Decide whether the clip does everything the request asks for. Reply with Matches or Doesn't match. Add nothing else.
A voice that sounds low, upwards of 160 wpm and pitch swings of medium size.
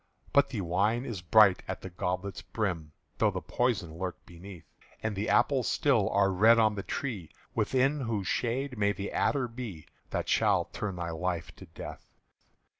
Matches